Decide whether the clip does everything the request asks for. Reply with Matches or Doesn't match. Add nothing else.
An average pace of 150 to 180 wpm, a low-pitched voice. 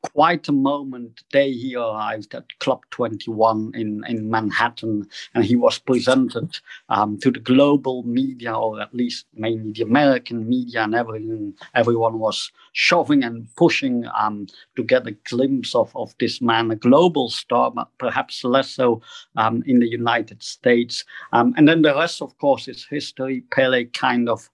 Matches